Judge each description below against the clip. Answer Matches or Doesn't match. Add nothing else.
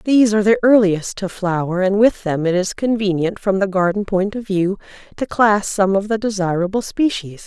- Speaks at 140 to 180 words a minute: Doesn't match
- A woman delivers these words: Matches